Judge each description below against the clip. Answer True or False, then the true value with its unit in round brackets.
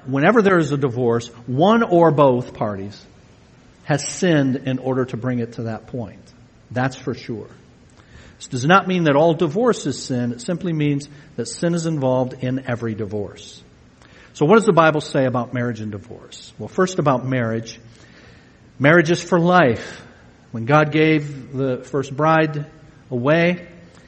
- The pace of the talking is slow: False (165 wpm)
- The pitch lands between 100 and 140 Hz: True (135 Hz)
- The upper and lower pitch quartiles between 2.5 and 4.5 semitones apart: False (4.9 semitones)